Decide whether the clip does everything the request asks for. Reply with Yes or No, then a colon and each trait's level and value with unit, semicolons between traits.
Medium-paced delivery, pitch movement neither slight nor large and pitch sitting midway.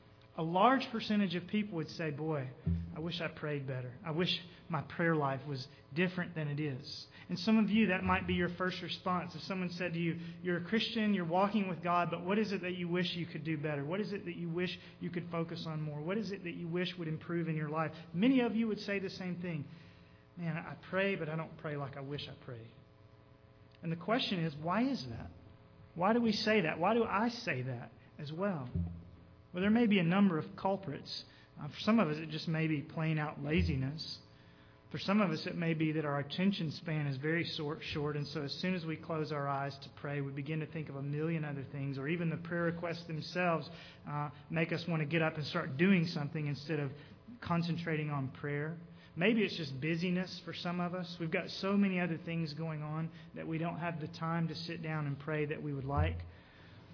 No: fast, 235 wpm; average, 3.2 semitones; medium, 165 Hz